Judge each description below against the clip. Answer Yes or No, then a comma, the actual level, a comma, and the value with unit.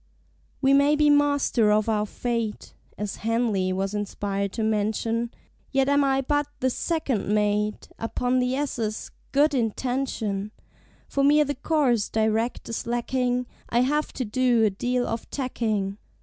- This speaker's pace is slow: No, average, 150 wpm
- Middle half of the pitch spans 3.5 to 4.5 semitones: Yes, average, 4.1 semitones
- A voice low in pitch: No, high, 235 Hz